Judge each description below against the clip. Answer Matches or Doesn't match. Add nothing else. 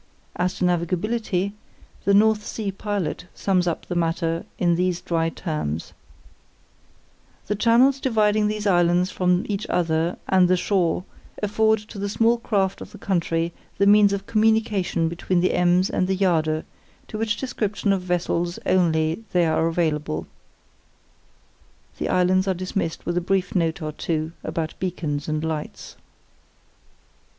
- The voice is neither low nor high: Matches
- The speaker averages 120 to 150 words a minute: Matches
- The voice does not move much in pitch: Doesn't match